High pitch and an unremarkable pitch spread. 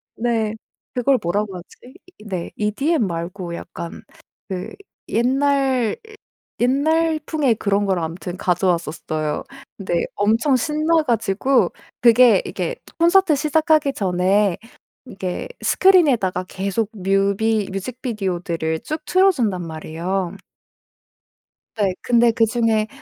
No: high, 215 Hz; wide, 6.4 semitones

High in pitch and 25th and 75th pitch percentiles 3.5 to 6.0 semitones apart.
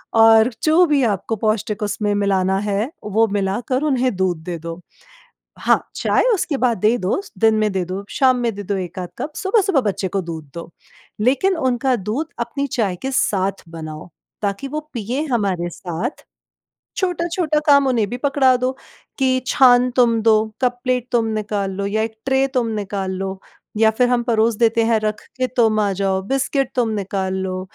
Yes: high, 225 Hz; average, 4.6 semitones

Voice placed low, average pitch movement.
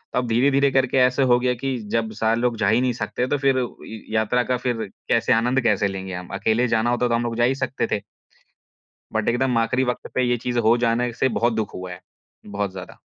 No: low, 120 Hz; narrow, 2.3 semitones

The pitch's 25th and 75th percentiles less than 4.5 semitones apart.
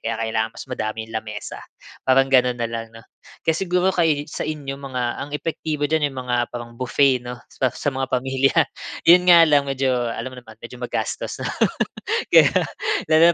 Yes: average, 3.5 semitones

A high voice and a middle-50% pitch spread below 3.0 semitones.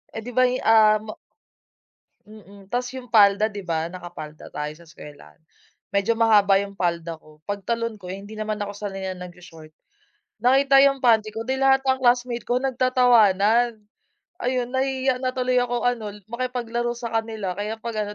No: high, 220 Hz; average, 3.9 semitones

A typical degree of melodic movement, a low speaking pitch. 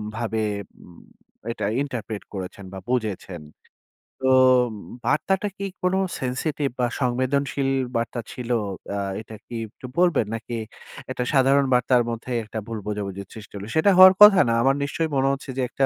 Yes: average, 4.0 semitones; low, 125 Hz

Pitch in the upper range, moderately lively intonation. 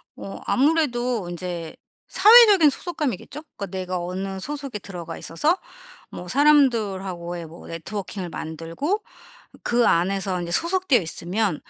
No: high, 195 Hz; wide, 8.5 semitones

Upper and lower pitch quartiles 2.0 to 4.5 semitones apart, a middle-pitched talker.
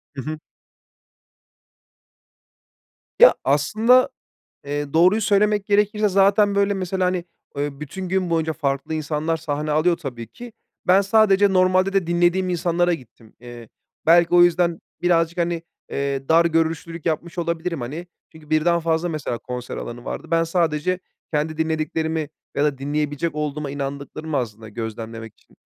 Yes: average, 3.7 semitones; medium, 165 Hz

